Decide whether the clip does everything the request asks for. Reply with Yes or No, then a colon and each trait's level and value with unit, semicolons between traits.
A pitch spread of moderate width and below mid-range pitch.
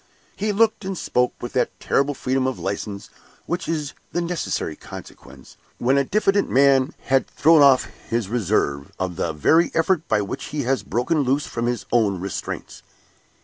No: wide, 6.2 semitones; low, 130 Hz